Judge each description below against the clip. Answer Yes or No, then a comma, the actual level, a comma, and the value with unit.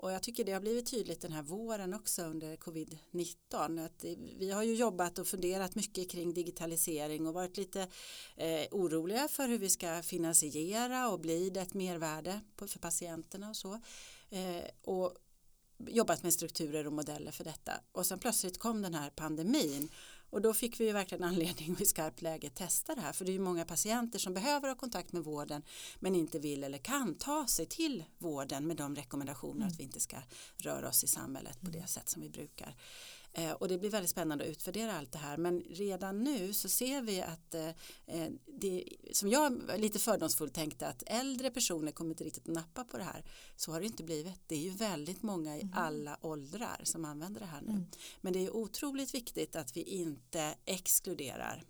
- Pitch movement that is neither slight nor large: Yes, average, 4.8 semitones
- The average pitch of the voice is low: No, medium, 180 Hz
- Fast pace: No, average, 195 wpm